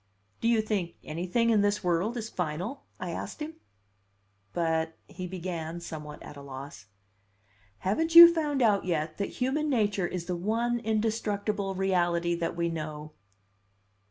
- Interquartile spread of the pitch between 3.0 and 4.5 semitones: No, average, 5.0 semitones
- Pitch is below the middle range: No, medium, 185 Hz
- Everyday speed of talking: Yes, average, 155 wpm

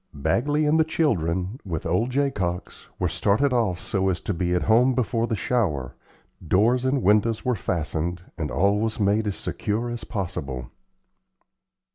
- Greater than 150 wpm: Yes, average, 160 wpm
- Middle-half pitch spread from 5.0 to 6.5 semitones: Yes, wide, 5.5 semitones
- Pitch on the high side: No, low, 105 Hz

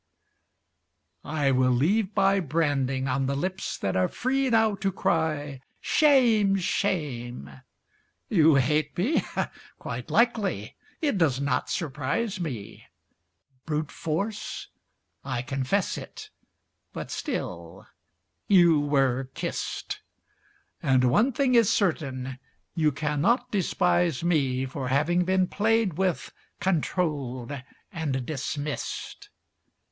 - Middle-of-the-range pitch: Yes, medium, 155 Hz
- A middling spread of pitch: No, wide, 6.4 semitones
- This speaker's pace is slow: Yes, slow, 105 wpm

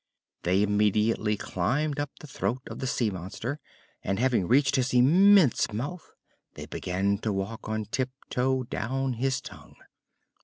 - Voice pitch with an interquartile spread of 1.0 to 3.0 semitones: No, average, 4.4 semitones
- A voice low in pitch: Yes, low, 120 Hz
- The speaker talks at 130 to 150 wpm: Yes, average, 145 wpm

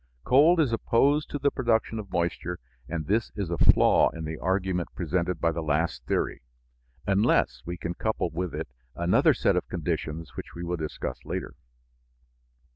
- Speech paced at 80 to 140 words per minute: No, average, 170 wpm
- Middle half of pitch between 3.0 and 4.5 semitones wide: No, average, 5.2 semitones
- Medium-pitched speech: No, very low, 90 Hz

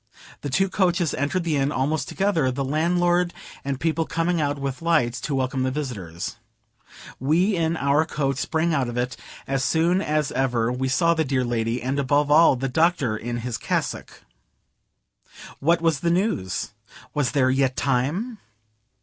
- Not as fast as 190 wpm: Yes, average, 165 wpm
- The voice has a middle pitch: Yes, medium, 145 Hz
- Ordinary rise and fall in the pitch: Yes, average, 4.4 semitones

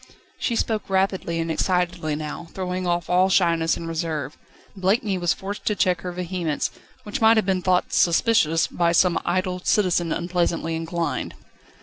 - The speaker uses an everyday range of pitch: No, narrow, 2.2 semitones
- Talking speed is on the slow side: No, average, 155 wpm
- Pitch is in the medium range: Yes, medium, 180 Hz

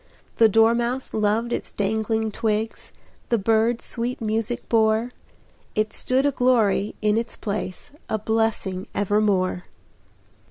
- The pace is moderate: No, slow, 120 wpm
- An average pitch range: No, narrow, 1.8 semitones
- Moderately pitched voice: No, high, 220 Hz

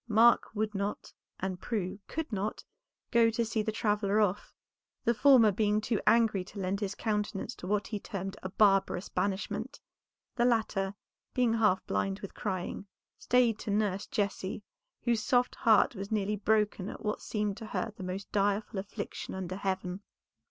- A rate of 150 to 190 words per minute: Yes, average, 165 wpm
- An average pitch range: No, narrow, 2.2 semitones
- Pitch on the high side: Yes, high, 210 Hz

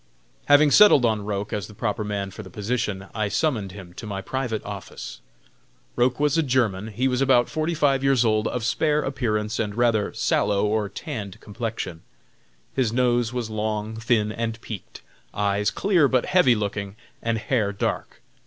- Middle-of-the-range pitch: No, low, 110 Hz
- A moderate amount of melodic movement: Yes, average, 3.7 semitones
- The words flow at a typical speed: Yes, average, 170 wpm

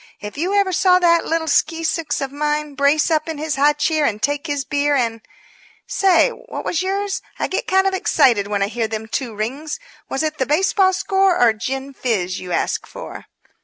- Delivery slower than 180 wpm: No, fast, 205 wpm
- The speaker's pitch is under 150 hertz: No, very high, 295 Hz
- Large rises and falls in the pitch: No, average, 4.9 semitones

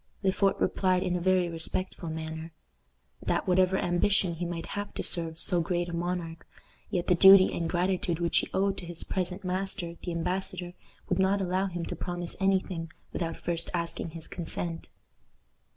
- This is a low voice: No, medium, 175 Hz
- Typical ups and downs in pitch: No, narrow, 1.8 semitones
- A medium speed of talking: Yes, average, 180 wpm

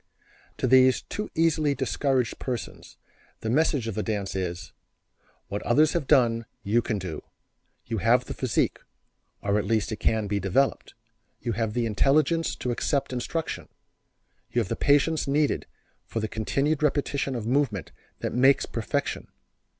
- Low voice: Yes, low, 120 Hz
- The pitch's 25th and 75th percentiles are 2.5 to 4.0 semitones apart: No, average, 4.5 semitones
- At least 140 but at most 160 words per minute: Yes, average, 155 wpm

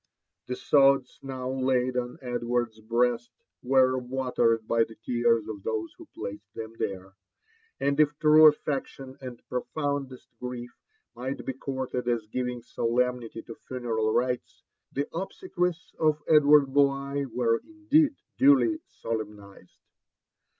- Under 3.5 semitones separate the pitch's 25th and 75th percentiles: Yes, average, 3.1 semitones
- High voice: No, low, 125 Hz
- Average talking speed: No, slow, 130 wpm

